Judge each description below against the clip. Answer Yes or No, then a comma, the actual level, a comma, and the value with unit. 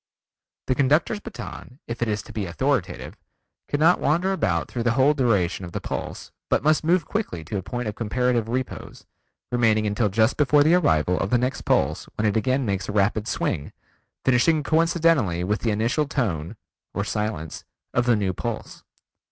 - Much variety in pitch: Yes, wide, 5.8 semitones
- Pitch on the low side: Yes, low, 120 Hz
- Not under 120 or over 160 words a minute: No, average, 180 wpm